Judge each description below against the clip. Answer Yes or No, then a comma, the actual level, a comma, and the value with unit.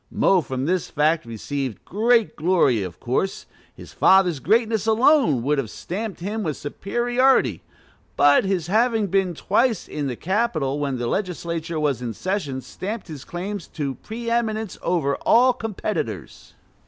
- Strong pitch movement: Yes, wide, 7.4 semitones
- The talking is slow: No, average, 150 wpm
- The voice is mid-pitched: Yes, medium, 180 Hz